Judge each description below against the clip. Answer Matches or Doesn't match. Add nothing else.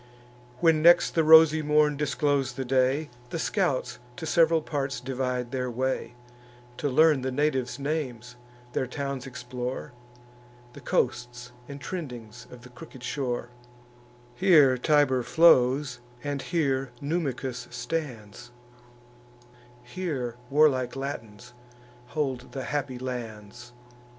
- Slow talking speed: Matches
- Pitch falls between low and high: Doesn't match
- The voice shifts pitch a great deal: Doesn't match